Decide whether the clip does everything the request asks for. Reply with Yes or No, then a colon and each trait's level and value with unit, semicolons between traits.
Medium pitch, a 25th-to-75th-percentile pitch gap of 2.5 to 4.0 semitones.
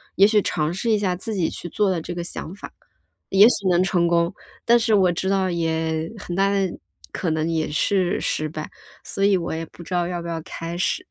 Yes: medium, 175 Hz; average, 2.9 semitones